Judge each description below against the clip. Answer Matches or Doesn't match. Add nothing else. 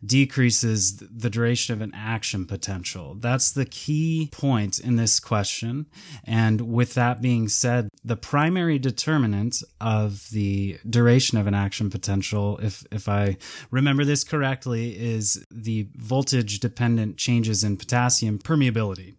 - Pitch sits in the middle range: Doesn't match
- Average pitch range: Matches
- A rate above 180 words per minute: Doesn't match